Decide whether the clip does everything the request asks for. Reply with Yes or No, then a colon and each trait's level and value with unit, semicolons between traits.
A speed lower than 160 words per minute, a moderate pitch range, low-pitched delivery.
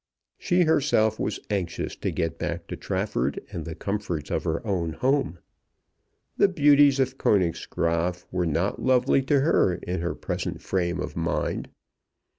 No: average, 150 wpm; wide, 8.0 semitones; very low, 95 Hz